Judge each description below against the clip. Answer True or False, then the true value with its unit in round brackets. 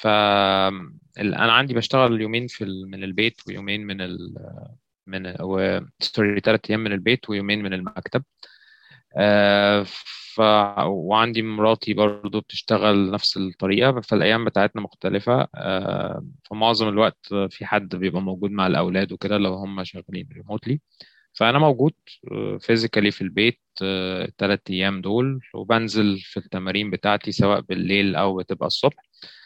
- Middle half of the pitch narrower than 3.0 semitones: True (2.6 semitones)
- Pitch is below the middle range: True (105 Hz)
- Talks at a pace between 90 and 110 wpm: False (120 wpm)